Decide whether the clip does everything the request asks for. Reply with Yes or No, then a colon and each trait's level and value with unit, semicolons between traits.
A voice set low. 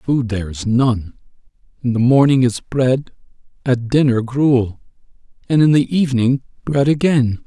Yes: low, 125 Hz